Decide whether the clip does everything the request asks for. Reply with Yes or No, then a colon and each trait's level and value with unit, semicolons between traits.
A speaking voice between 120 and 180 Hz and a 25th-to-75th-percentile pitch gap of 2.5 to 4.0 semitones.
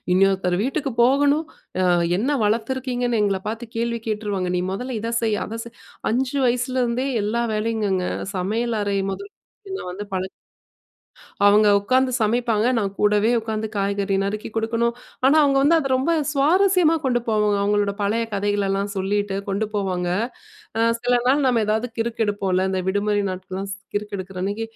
No: high, 220 Hz; average, 3.5 semitones